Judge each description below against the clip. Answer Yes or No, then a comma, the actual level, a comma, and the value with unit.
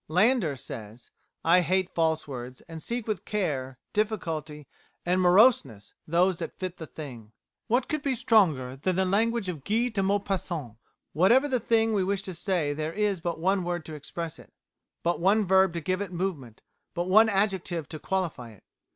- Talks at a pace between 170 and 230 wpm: Yes, average, 180 wpm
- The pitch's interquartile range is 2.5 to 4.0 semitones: No, average, 4.6 semitones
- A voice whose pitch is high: No, medium, 180 Hz